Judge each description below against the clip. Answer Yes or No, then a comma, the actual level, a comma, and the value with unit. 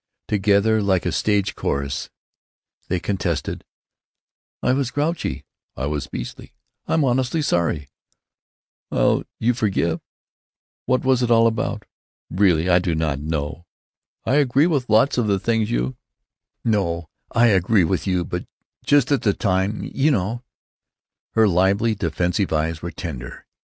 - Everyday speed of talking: No, slow, 130 wpm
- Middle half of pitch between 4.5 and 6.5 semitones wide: Yes, wide, 5.6 semitones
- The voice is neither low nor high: No, low, 100 Hz